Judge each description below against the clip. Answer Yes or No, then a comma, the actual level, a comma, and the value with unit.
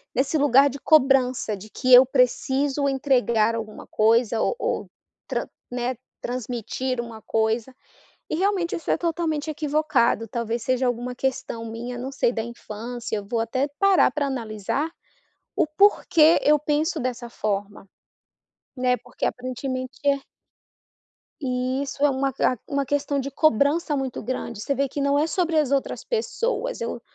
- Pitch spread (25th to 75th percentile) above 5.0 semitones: No, average, 3.5 semitones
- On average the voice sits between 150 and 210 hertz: No, very high, 260 Hz